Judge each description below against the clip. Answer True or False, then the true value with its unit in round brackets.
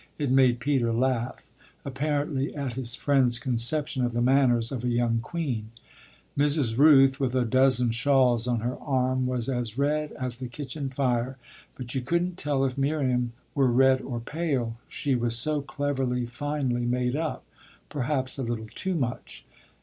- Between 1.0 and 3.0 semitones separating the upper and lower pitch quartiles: True (2.7 semitones)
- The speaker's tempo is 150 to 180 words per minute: True (165 wpm)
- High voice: False (130 Hz)